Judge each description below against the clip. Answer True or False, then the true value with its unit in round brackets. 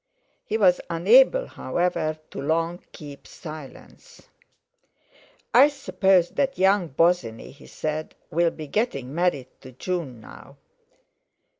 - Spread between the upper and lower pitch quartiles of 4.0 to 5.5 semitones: True (4.3 semitones)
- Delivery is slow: True (115 wpm)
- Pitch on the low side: False (170 Hz)